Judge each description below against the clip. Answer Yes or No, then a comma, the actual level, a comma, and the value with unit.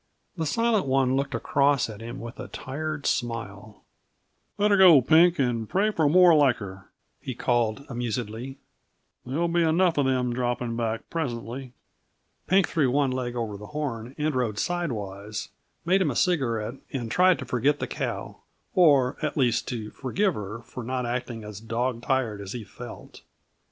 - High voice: No, low, 125 Hz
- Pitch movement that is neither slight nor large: Yes, average, 4.8 semitones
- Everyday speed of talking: Yes, average, 170 wpm